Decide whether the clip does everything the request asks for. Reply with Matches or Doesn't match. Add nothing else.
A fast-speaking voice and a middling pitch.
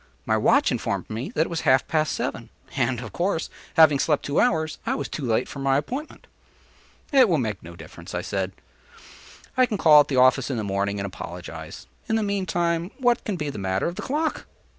Matches